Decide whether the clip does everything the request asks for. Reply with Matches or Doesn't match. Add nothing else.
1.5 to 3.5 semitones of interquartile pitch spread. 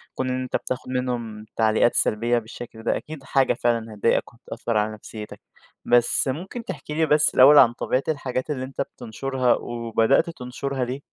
Matches